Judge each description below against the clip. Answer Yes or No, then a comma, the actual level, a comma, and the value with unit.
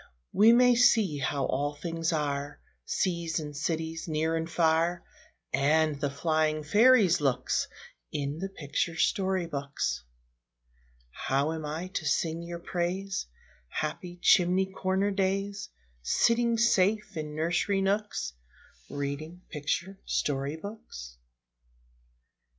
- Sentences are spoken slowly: Yes, slow, 115 wpm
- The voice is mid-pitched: Yes, medium, 165 Hz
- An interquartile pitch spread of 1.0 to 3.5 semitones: No, average, 4.5 semitones